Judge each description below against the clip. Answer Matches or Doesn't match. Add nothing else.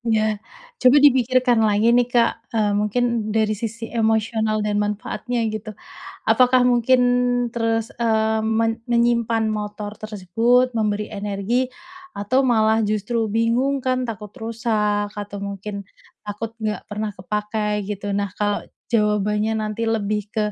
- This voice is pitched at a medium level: Doesn't match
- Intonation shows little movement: Matches